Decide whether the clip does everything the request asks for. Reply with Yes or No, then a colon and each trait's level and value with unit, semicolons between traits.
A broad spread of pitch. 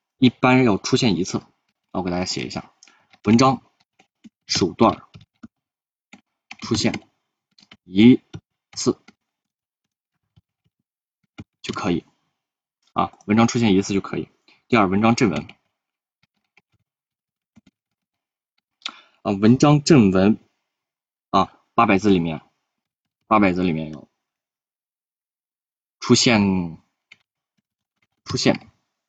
No: average, 4.7 semitones